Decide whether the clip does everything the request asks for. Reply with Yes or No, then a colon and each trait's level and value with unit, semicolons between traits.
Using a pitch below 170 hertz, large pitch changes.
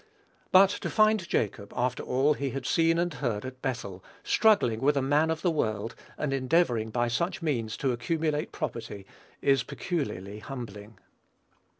Yes: low, 135 Hz; wide, 5.9 semitones